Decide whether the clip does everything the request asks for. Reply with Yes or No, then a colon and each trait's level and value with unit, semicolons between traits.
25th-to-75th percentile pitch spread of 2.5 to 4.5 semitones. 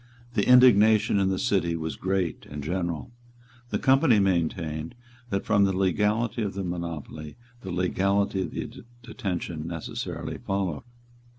Yes: average, 3.2 semitones